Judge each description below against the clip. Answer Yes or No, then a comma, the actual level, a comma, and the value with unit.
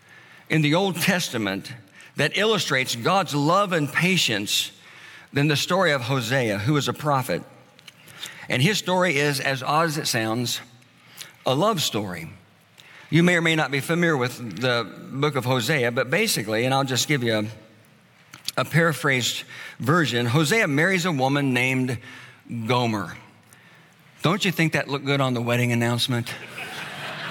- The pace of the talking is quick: No, average, 155 wpm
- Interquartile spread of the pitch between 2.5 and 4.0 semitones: No, average, 4.9 semitones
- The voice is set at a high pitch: No, medium, 140 Hz